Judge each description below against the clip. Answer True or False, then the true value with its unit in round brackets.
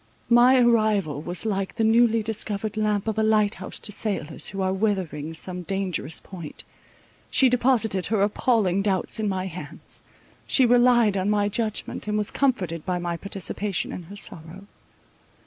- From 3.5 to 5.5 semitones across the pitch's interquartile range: False (3.0 semitones)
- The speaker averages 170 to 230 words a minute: False (160 wpm)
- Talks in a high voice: True (205 Hz)